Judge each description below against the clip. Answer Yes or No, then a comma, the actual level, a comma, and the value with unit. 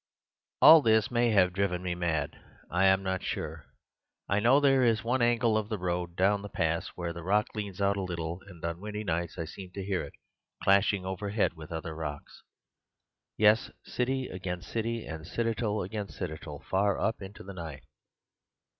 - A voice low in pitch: Yes, very low, 95 Hz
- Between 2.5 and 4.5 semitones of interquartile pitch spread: Yes, average, 3.8 semitones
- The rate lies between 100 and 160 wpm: No, average, 180 wpm